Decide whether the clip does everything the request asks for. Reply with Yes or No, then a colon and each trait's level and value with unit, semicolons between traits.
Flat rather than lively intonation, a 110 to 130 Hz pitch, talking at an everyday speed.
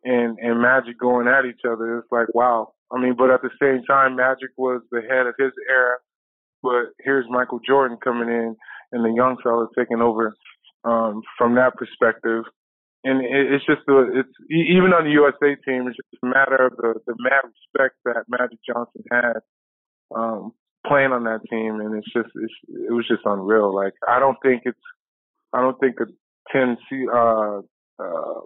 Yes: narrow, 2.1 semitones; low, 125 Hz; average, 190 wpm